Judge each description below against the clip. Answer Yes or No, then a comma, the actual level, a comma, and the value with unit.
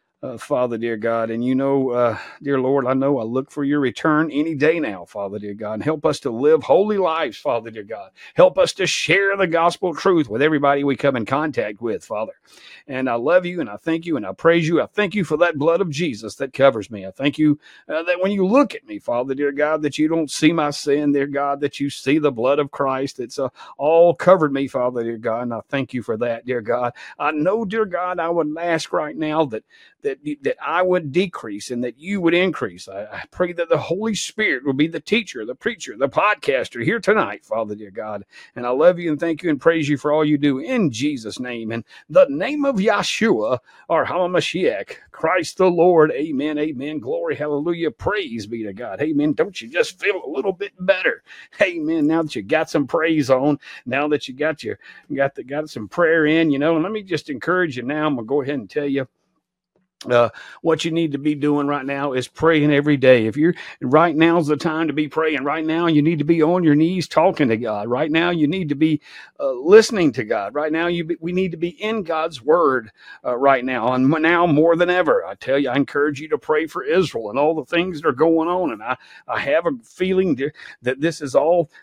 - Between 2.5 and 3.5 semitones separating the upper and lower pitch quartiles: No, average, 4.0 semitones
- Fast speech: Yes, fast, 240 wpm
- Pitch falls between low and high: Yes, medium, 155 Hz